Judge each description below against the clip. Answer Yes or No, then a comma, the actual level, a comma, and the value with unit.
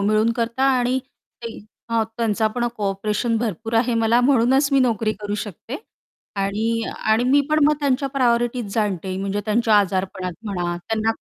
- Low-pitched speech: No, high, 225 Hz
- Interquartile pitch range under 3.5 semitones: Yes, average, 2.9 semitones